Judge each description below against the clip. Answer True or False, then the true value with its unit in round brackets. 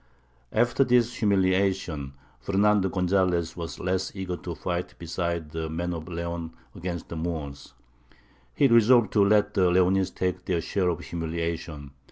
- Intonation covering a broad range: False (2.6 semitones)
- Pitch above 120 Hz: False (90 Hz)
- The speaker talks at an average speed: True (145 wpm)